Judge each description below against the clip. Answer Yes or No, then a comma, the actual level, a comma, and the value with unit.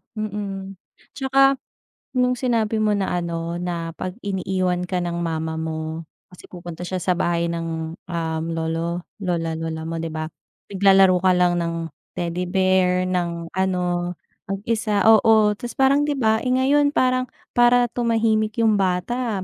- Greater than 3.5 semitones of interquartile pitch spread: Yes, average, 4.5 semitones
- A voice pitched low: No, medium, 185 Hz